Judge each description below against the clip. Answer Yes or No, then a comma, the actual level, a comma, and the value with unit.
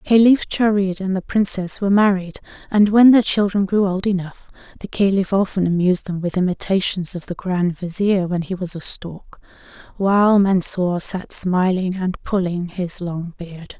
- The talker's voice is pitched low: No, high, 190 Hz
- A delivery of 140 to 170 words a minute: Yes, average, 165 wpm